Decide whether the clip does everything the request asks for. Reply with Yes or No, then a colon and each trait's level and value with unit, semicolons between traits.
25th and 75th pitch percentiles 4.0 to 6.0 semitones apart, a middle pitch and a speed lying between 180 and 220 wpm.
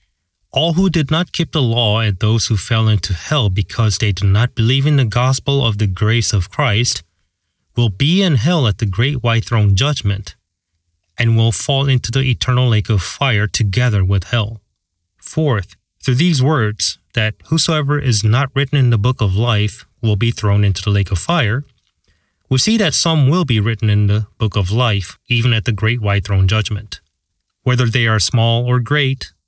No: average, 4.3 semitones; low, 115 Hz; average, 195 wpm